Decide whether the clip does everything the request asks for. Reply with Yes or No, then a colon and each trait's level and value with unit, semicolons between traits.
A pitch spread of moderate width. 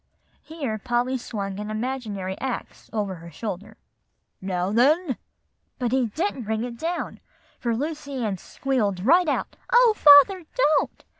No: wide, 5.7 semitones